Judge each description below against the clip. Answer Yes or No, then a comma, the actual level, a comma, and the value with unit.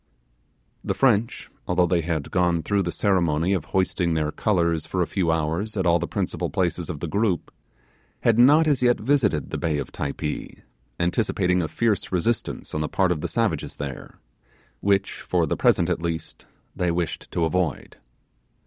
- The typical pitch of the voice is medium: No, very low, 90 Hz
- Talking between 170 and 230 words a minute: Yes, average, 175 wpm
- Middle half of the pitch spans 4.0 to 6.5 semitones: No, average, 3.5 semitones